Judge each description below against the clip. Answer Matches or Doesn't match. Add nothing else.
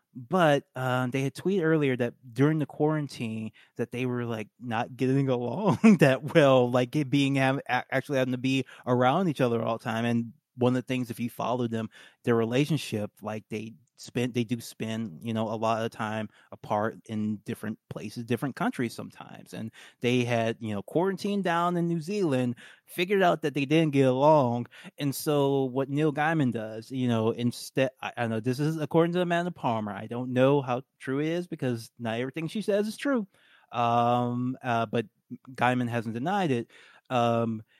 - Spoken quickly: Doesn't match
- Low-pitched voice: Matches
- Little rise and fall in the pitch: Doesn't match